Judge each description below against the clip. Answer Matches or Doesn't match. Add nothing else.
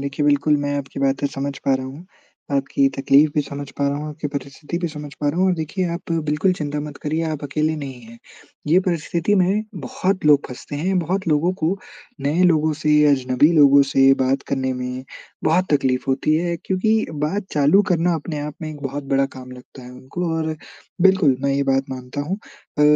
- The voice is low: Doesn't match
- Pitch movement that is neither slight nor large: Matches